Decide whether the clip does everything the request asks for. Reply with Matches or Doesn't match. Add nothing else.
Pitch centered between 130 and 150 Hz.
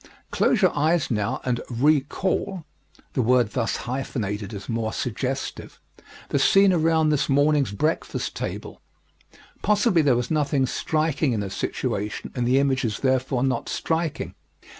Matches